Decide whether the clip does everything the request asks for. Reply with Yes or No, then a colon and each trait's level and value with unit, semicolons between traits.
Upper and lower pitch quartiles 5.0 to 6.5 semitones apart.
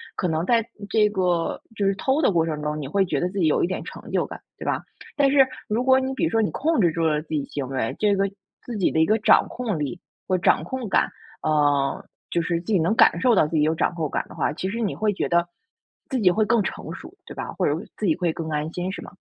Yes: average, 5.3 semitones